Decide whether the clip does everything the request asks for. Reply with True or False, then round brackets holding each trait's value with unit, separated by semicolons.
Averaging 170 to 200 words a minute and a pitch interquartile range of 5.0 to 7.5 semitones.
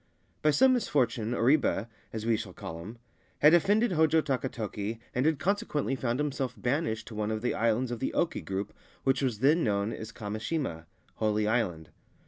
True (180 wpm; 5.5 semitones)